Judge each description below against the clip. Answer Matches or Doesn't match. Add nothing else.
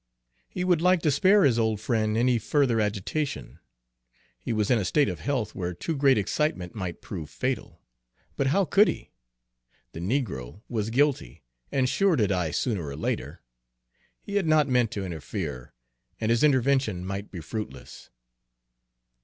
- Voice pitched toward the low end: Matches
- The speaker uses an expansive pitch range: Matches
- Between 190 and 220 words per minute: Doesn't match